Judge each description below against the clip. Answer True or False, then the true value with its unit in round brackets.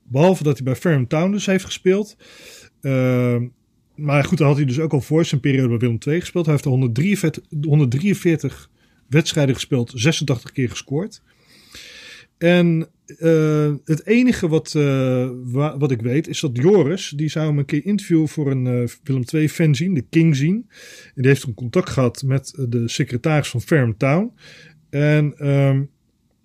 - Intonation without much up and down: False (4.0 semitones)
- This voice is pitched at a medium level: True (150 Hz)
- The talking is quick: False (175 wpm)